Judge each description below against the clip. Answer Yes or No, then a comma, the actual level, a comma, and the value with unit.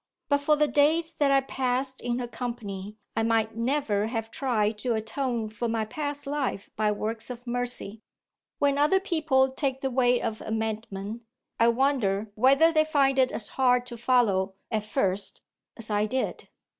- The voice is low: No, high, 245 Hz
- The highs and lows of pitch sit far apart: No, average, 3.8 semitones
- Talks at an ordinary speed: Yes, average, 170 wpm